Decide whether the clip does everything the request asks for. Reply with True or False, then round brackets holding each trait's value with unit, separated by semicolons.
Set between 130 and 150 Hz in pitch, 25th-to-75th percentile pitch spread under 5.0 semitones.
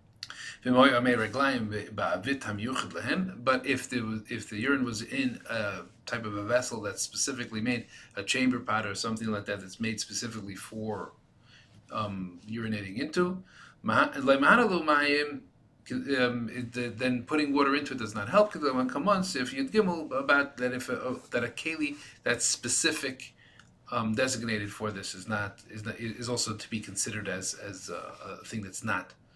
False (120 Hz; 4.0 semitones)